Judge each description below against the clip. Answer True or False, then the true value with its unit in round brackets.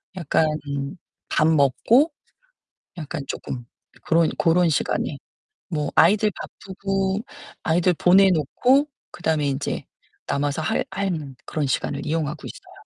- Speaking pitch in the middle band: True (165 Hz)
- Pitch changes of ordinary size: True (4.6 semitones)